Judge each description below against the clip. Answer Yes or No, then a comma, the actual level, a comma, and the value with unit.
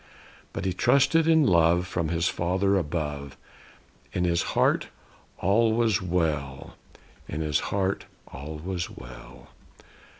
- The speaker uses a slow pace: Yes, slow, 125 wpm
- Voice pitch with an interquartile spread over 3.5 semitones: Yes, average, 4.2 semitones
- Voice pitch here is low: Yes, very low, 90 Hz